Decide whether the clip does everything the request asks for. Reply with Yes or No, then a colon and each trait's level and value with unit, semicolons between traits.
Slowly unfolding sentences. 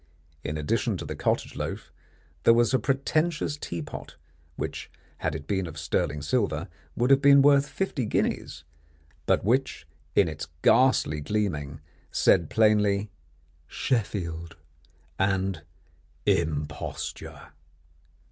Yes: slow, 120 wpm